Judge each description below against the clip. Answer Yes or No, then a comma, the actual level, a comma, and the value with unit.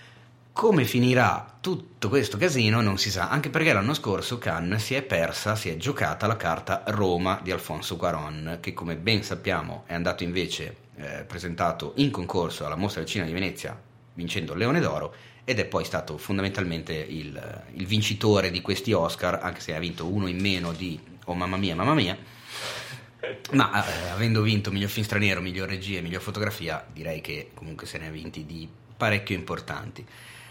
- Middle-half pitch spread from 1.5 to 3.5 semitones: No, average, 3.9 semitones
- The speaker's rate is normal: No, fast, 180 wpm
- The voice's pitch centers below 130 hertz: Yes, very low, 95 Hz